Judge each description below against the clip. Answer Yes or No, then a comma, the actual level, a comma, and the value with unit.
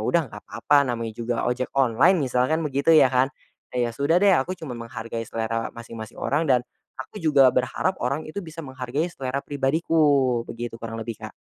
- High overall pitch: No, low, 130 Hz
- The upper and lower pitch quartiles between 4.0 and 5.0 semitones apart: Yes, average, 4.7 semitones